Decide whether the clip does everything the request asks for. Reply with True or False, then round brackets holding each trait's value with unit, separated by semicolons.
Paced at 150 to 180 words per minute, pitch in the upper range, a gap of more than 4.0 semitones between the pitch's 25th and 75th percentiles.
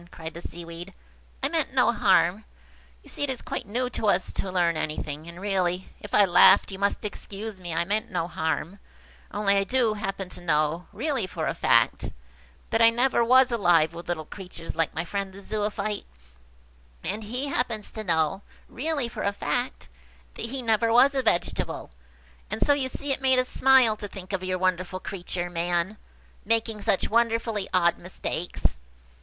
True (170 wpm; 200 Hz; 4.7 semitones)